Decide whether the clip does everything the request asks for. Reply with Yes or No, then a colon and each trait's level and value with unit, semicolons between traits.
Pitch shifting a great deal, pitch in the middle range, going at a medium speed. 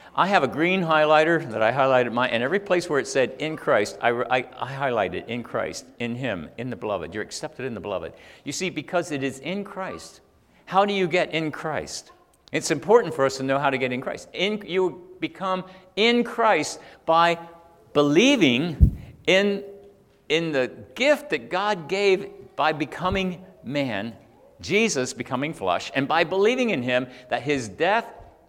Yes: wide, 6.4 semitones; medium, 170 Hz; average, 180 wpm